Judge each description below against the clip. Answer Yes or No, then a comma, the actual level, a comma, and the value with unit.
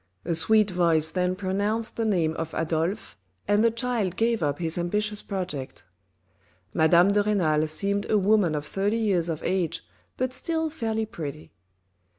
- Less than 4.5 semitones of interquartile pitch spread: No, average, 4.8 semitones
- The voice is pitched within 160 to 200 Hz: Yes, high, 190 Hz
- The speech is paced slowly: No, average, 160 wpm